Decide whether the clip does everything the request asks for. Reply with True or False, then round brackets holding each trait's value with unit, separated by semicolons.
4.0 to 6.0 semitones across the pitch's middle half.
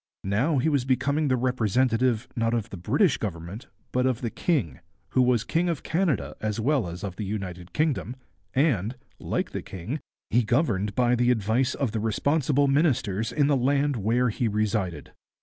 True (4.8 semitones)